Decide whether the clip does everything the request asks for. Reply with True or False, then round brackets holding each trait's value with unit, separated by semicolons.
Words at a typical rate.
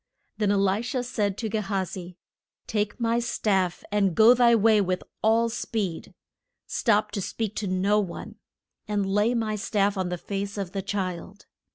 True (180 wpm)